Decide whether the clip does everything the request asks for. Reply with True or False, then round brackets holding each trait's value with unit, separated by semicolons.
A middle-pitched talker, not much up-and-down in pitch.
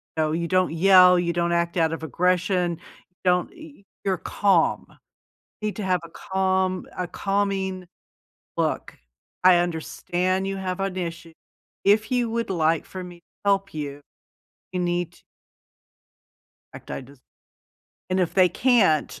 True (180 Hz; 2.0 semitones)